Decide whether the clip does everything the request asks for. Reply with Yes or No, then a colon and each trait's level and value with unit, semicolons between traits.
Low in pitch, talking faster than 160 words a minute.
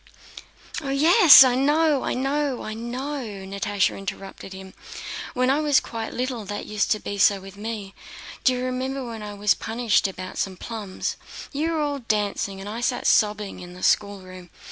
No: high, 225 Hz; average, 185 wpm